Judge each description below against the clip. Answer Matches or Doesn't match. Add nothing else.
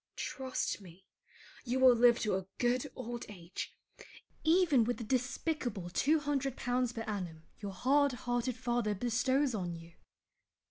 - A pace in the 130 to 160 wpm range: Matches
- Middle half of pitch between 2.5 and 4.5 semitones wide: Matches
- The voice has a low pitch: Doesn't match